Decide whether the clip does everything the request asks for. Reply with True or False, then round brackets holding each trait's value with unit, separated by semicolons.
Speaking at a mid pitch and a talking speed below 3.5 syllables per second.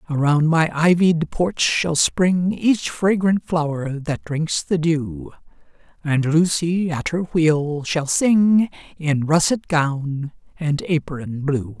True (160 Hz; 3.2 syllables/s)